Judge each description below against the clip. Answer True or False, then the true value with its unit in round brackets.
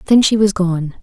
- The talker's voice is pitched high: True (195 Hz)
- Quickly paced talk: True (235 wpm)